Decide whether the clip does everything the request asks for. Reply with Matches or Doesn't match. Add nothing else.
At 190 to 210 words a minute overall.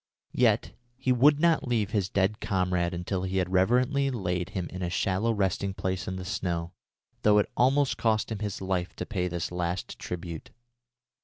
Doesn't match